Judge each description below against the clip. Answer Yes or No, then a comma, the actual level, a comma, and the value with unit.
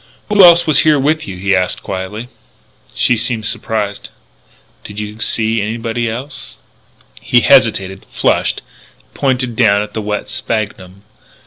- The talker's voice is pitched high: No, low, 110 Hz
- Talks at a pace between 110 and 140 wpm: Yes, slow, 135 wpm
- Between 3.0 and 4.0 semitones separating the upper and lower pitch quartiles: Yes, average, 3.4 semitones